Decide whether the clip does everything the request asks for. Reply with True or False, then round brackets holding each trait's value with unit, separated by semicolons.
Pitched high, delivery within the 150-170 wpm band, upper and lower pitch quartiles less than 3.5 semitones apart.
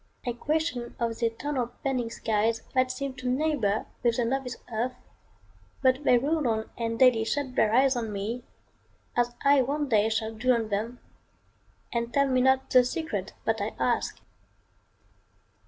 True (245 Hz; 165 wpm; 2.7 semitones)